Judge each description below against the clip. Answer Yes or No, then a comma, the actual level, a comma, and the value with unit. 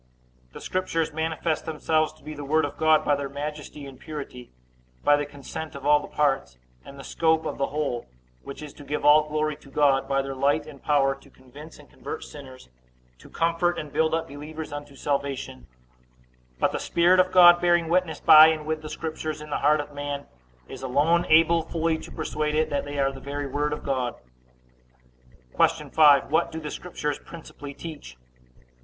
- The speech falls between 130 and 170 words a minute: No, average, 200 wpm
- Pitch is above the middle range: No, medium, 150 Hz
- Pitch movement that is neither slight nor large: No, narrow, 2.2 semitones